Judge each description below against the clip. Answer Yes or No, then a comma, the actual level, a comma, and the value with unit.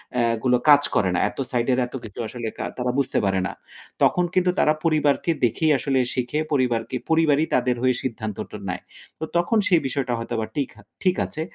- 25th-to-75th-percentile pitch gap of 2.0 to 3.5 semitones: No, average, 4.1 semitones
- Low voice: Yes, low, 130 Hz